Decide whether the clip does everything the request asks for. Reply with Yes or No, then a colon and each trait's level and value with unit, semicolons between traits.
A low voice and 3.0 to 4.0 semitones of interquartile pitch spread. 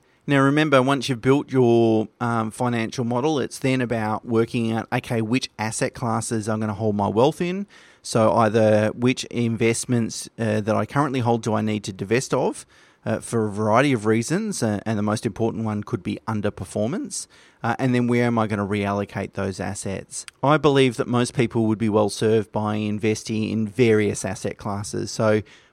No: low, 115 Hz; narrow, 2.6 semitones